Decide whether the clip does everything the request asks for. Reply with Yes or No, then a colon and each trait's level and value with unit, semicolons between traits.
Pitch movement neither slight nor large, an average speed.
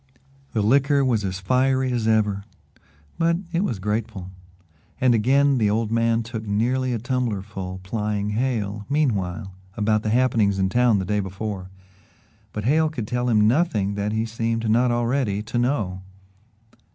Yes: average, 3.6 semitones; average, 160 wpm